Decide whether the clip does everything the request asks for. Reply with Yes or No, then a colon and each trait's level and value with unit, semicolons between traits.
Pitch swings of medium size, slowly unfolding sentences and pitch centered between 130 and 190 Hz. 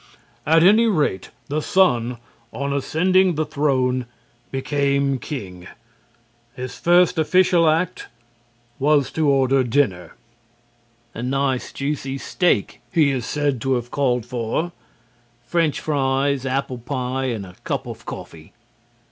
Yes: average, 3.6 semitones; slow, 120 wpm; medium, 140 Hz